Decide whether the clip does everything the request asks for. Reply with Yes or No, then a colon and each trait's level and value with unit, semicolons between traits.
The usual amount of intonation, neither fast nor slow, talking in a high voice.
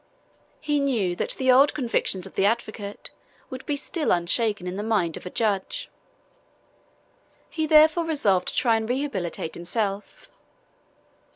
No: wide, 6.5 semitones; average, 145 wpm; high, 225 Hz